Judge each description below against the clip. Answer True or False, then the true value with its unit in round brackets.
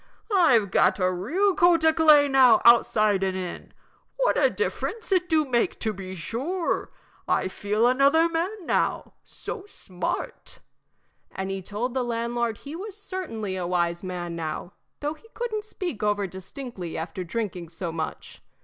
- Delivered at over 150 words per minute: True (160 wpm)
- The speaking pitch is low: False (235 Hz)